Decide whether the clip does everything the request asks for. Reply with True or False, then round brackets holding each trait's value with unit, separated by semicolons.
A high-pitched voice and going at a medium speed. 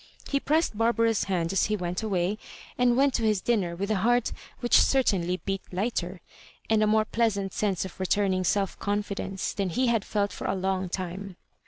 True (200 Hz; 190 wpm)